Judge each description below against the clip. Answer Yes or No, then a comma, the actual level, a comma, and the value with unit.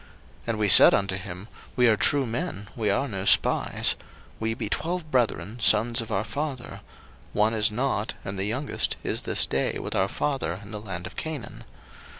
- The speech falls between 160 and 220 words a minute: Yes, average, 195 wpm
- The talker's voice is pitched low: Yes, low, 110 Hz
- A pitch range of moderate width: Yes, average, 4.1 semitones